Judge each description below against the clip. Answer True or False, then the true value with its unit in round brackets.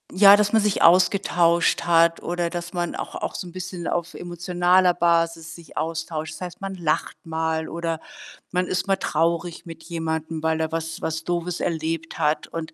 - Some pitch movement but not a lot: False (1.6 semitones)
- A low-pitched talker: False (170 Hz)